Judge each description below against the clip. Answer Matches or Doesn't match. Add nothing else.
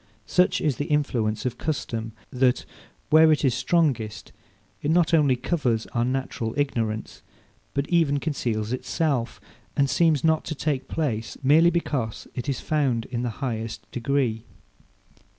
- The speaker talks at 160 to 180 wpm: Doesn't match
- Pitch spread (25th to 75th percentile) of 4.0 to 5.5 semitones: Matches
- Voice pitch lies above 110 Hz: Matches